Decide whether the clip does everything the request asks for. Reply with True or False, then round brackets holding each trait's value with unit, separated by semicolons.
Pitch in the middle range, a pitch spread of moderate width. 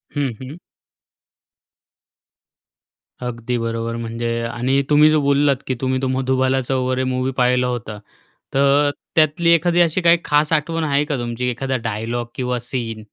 False (130 Hz; 3.4 semitones)